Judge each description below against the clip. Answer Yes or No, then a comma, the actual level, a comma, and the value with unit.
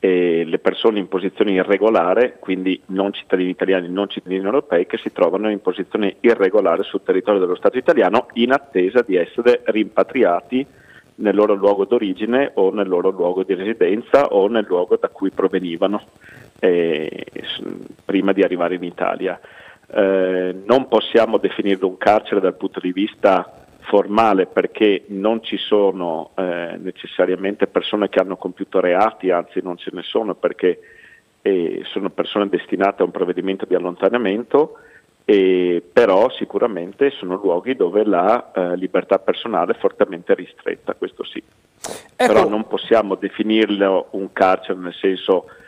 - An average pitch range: No, wide, 7.0 semitones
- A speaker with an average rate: Yes, average, 145 wpm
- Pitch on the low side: Yes, low, 100 Hz